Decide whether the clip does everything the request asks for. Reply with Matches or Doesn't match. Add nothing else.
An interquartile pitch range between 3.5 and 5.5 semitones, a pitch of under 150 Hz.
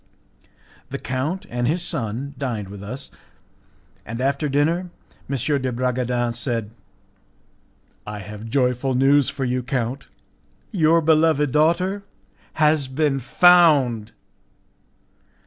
Matches